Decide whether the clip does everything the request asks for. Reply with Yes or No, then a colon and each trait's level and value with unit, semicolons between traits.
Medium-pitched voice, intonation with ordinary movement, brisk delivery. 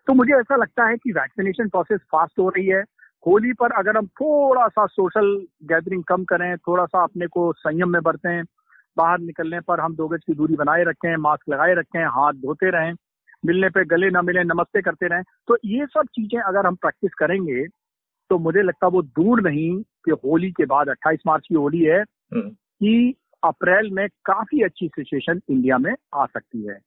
Yes: medium, 180 Hz; average, 4.1 semitones; fast, 195 wpm